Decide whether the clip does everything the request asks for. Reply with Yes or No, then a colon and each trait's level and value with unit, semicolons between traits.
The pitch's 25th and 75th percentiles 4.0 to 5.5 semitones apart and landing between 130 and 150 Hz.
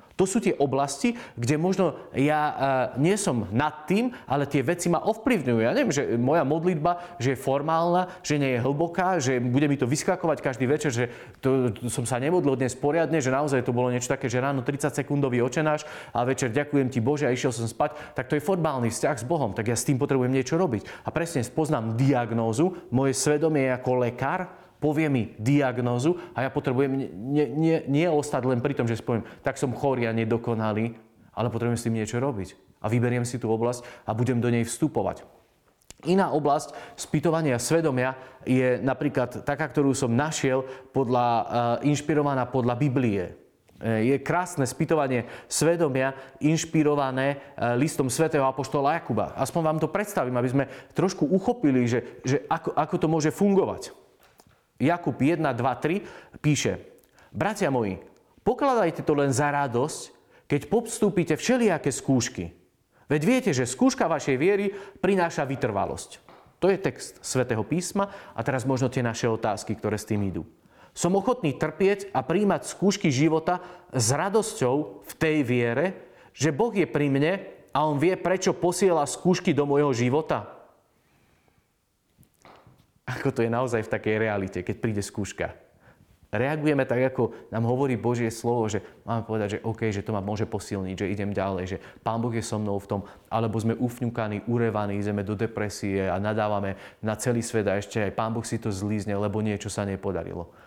Yes: average, 5.1 semitones; low, 135 Hz